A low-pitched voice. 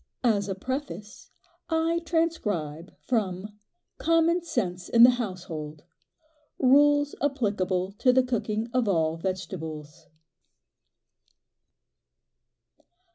No: high, 210 Hz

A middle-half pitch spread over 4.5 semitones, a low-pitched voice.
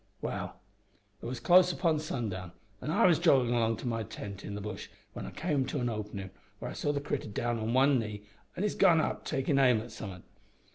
Yes: wide, 5.6 semitones; low, 120 Hz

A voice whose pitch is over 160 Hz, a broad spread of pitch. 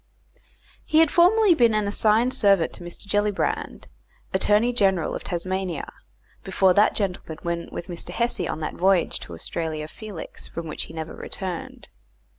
No: high, 190 Hz; average, 4.1 semitones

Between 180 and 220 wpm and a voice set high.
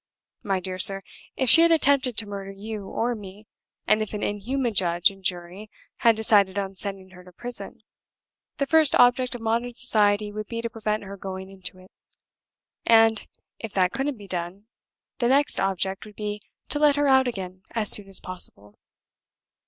Yes: average, 185 wpm; high, 210 Hz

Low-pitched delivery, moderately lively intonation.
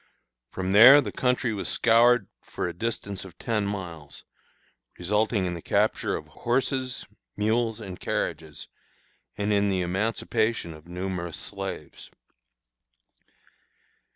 Yes: low, 100 Hz; average, 4.3 semitones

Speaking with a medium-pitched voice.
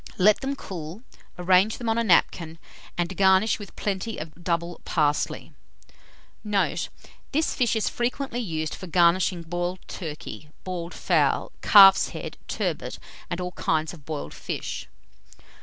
Yes: medium, 180 Hz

